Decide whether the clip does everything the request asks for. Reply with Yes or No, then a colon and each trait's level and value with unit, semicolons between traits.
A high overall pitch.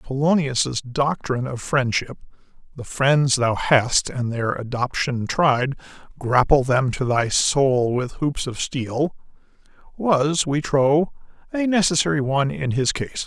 No: low, 135 Hz